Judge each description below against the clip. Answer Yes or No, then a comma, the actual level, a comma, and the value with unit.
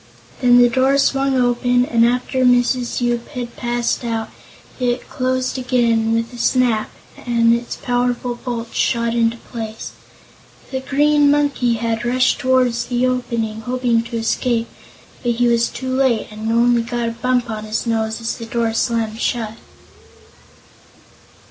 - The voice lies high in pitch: Yes, high, 240 Hz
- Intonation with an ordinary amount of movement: No, narrow, 1.6 semitones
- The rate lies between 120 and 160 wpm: Yes, average, 150 wpm